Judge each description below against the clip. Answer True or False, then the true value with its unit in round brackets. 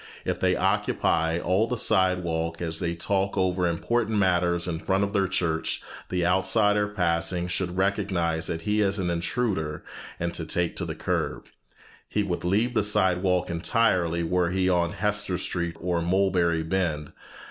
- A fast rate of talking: False (160 wpm)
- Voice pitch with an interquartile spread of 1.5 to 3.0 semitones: True (2.6 semitones)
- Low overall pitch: True (90 Hz)